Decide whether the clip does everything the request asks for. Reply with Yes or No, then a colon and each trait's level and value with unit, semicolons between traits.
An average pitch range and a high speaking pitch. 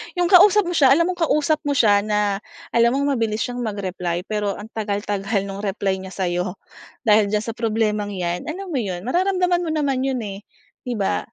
No: wide, 6.0 semitones; high, 215 Hz